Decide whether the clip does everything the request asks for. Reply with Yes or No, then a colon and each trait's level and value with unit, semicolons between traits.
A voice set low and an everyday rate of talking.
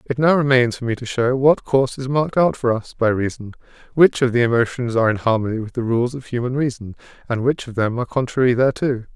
No: low, 125 Hz; fast, 235 wpm